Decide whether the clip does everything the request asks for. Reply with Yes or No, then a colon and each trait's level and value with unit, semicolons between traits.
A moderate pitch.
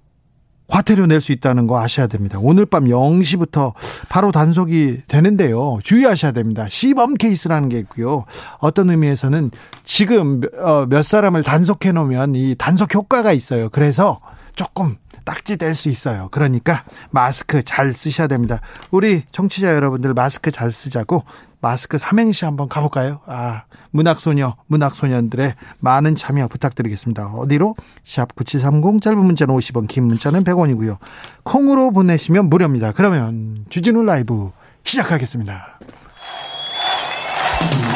Yes: medium, 145 Hz